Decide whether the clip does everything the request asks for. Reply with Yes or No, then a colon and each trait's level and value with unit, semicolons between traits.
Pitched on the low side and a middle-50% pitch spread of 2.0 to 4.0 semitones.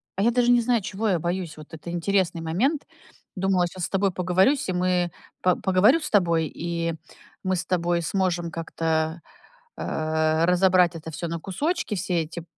No: medium, 180 Hz; narrow, 2.5 semitones